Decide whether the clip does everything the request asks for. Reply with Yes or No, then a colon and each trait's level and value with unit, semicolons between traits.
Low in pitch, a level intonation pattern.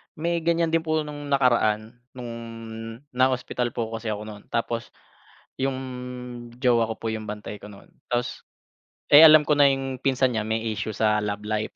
No: low, 120 Hz; average, 4.2 semitones